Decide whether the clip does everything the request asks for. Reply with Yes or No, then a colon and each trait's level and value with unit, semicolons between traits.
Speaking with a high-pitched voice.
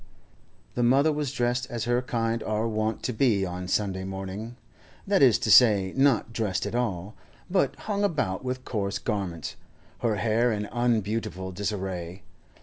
No: low, 110 Hz